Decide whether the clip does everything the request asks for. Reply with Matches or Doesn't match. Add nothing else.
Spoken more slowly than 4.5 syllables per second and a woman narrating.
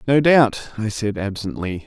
Doesn't match